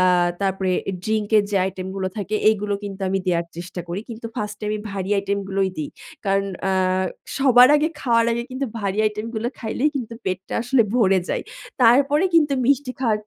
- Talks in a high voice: Yes, high, 210 Hz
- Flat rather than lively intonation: No, average, 3.8 semitones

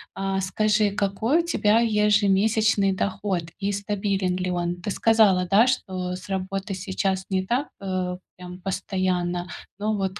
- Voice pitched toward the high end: Yes, high, 195 Hz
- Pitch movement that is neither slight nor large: No, narrow, 2.1 semitones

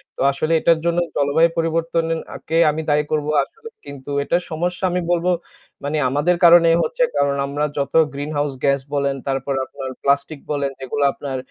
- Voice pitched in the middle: Yes, medium, 150 Hz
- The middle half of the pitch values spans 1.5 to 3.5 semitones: Yes, average, 2.8 semitones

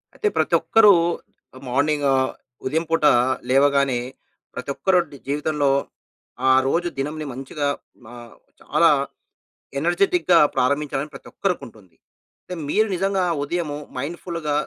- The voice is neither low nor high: Yes, medium, 150 Hz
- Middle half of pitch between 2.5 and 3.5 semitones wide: No, average, 3.9 semitones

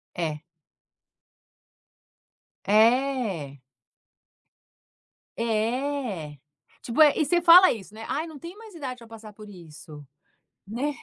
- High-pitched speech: Yes, high, 230 Hz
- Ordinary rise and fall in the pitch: No, wide, 6.7 semitones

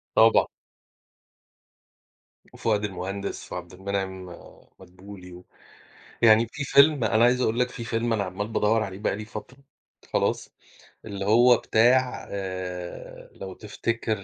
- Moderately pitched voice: No, low, 105 Hz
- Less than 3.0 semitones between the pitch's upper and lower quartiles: No, average, 3.4 semitones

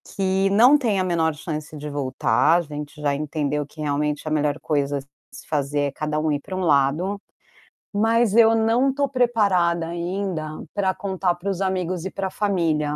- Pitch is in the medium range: Yes, medium, 170 Hz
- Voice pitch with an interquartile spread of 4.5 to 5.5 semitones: Yes, average, 4.8 semitones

